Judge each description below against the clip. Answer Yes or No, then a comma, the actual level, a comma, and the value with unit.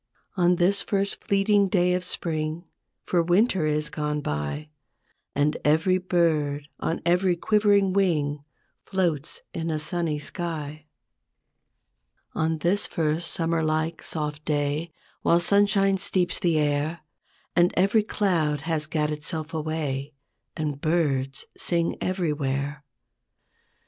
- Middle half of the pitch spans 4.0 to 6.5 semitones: No, average, 3.1 semitones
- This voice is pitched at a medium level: Yes, medium, 160 Hz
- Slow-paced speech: Yes, slow, 120 wpm